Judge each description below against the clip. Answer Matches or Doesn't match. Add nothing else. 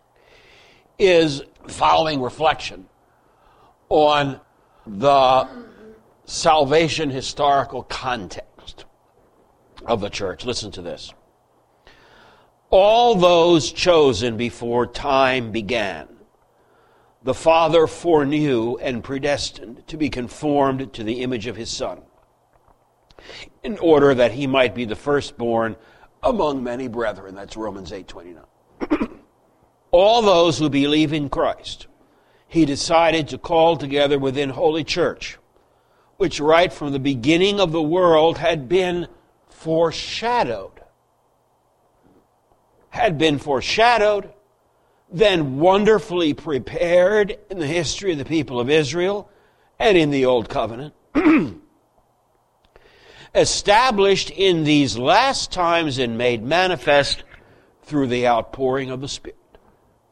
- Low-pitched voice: Doesn't match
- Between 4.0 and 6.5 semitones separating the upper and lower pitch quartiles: Matches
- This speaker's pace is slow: Matches